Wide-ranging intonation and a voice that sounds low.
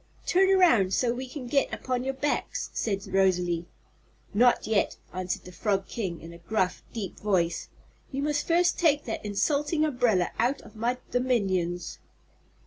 No: wide, 6.4 semitones; high, 230 Hz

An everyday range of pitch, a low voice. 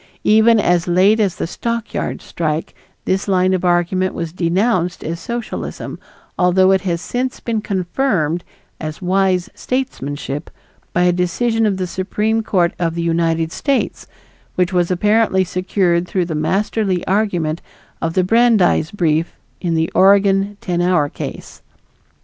No: average, 3.2 semitones; medium, 185 Hz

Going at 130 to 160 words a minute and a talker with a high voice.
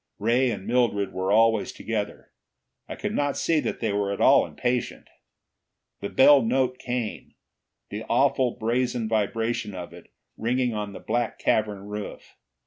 No: average, 150 wpm; low, 115 Hz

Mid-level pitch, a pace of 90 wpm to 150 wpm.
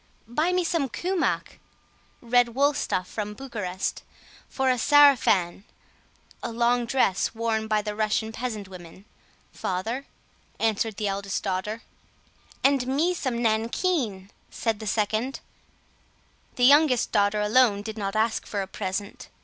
No: high, 225 Hz; slow, 135 wpm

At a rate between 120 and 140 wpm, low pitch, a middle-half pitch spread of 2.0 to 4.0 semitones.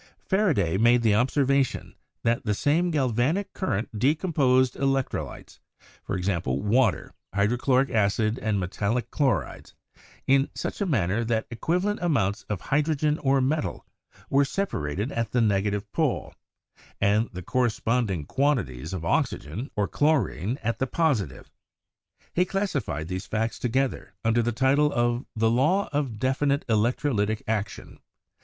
No: slow, 135 wpm; low, 120 Hz; average, 5.1 semitones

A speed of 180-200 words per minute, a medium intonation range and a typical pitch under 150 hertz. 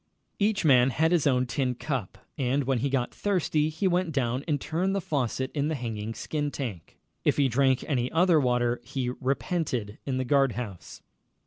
Yes: average, 190 wpm; average, 4.1 semitones; low, 135 Hz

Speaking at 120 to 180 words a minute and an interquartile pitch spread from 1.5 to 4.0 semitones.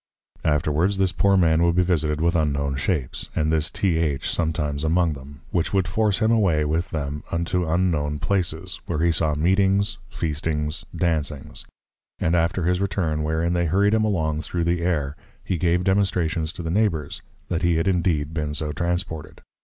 Yes: average, 175 wpm; average, 2.9 semitones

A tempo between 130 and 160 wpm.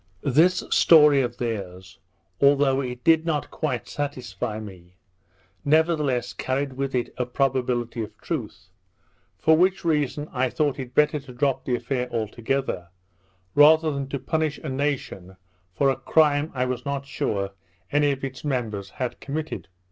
Yes: average, 150 wpm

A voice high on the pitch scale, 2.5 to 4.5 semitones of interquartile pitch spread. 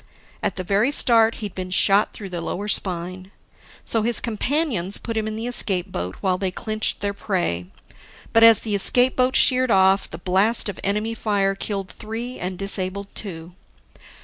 Yes: high, 200 Hz; average, 3.3 semitones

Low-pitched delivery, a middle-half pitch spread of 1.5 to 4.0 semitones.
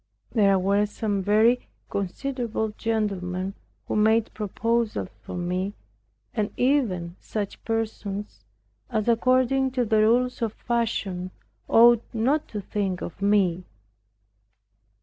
No: high, 215 Hz; average, 3.1 semitones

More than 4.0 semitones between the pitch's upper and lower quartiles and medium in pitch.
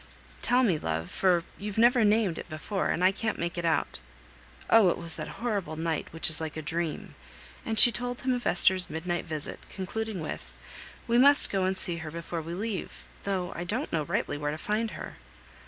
Yes: average, 5.2 semitones; medium, 180 Hz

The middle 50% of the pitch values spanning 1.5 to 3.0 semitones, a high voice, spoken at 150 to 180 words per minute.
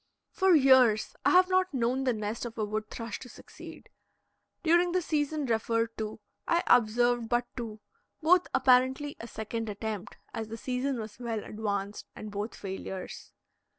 No: average, 3.7 semitones; high, 235 Hz; average, 160 wpm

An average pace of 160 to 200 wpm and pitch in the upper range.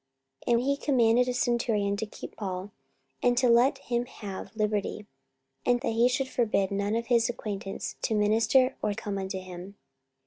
Yes: average, 175 wpm; high, 225 Hz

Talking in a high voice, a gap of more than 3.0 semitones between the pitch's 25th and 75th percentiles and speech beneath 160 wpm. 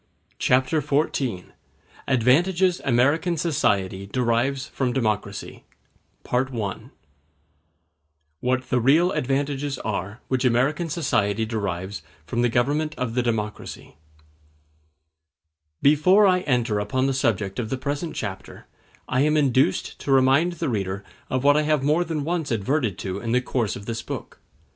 No: low, 130 Hz; average, 4.6 semitones; slow, 135 wpm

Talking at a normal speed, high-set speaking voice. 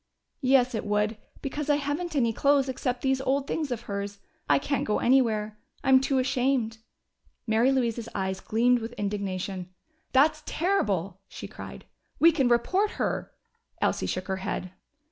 Yes: average, 160 wpm; high, 245 Hz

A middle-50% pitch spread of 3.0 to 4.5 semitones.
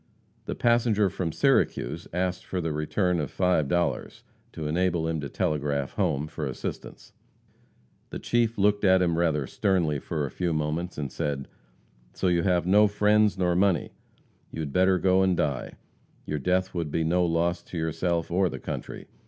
Yes: average, 3.4 semitones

